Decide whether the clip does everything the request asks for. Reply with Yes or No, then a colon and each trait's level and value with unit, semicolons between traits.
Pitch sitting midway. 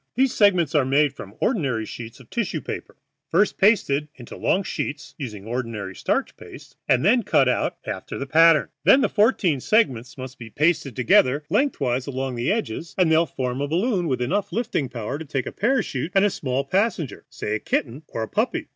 Yes: medium, 145 Hz